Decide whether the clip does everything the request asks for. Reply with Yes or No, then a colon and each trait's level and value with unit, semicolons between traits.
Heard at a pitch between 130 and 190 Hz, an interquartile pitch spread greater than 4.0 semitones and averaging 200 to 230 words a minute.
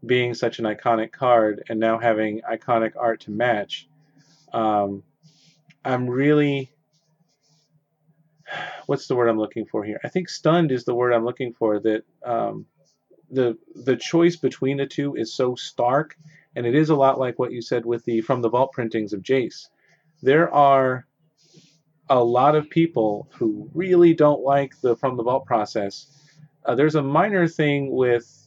No: low, 135 Hz; average, 4.8 semitones; average, 170 wpm